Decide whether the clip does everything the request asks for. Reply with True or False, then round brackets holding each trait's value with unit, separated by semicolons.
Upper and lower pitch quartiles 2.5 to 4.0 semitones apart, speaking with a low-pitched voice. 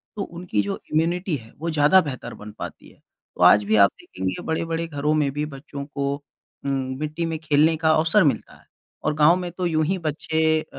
False (2.9 semitones; 155 Hz)